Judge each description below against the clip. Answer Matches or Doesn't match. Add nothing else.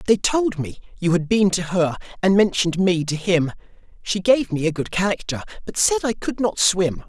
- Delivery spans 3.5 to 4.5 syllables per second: Doesn't match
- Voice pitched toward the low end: Doesn't match